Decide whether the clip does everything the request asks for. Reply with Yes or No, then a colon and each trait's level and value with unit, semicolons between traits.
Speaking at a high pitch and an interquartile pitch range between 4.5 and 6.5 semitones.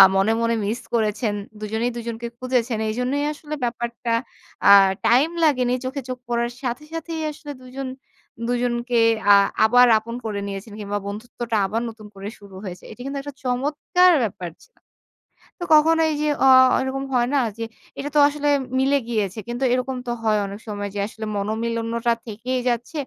No: high, 240 Hz; average, 3.3 semitones